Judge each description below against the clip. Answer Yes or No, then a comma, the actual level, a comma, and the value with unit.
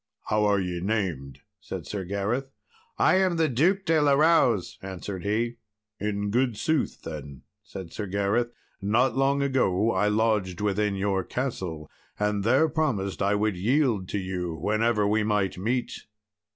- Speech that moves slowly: No, average, 155 wpm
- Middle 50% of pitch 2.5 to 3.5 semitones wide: No, average, 4.5 semitones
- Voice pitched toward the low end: Yes, low, 105 Hz